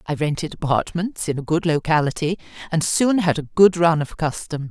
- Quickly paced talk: No, average, 190 wpm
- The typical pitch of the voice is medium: Yes, medium, 160 Hz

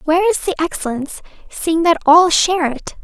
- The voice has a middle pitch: No, very high, 330 Hz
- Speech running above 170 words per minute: Yes, average, 180 wpm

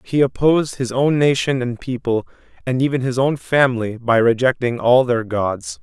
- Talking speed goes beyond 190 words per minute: No, average, 175 wpm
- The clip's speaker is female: No, male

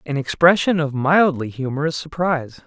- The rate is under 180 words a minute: Yes, slow, 135 wpm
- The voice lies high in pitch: No, medium, 150 Hz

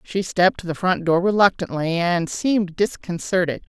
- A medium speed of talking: Yes, average, 160 wpm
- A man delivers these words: No, female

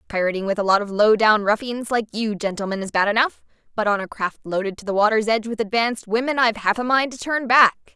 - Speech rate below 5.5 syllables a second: No, 6.4 syllables/s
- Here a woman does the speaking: Yes, female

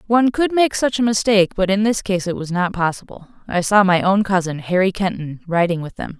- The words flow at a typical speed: No, fast, 235 wpm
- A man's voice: No, female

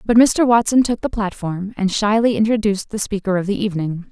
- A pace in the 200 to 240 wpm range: Yes, fast, 205 wpm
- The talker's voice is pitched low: No, high, 210 Hz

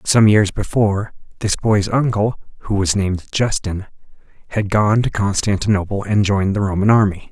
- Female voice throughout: No, male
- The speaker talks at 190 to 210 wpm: No, average, 155 wpm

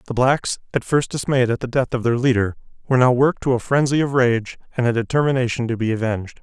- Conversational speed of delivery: No, fast, 235 wpm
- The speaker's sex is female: No, male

